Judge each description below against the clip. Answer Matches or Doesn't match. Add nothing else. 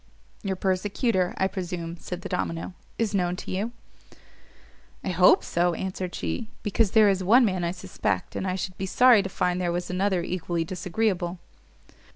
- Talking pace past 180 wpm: Doesn't match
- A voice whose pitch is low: Doesn't match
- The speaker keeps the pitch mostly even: Matches